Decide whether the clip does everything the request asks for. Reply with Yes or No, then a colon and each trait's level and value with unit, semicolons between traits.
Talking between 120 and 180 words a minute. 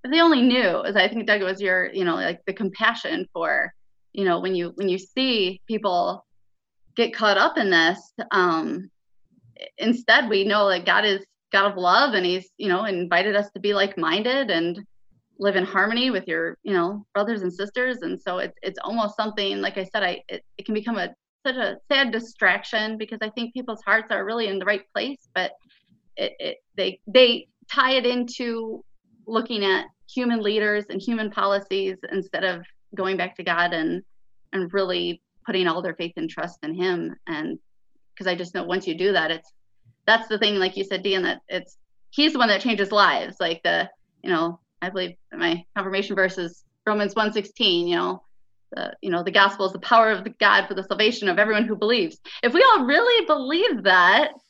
No: fast, 205 wpm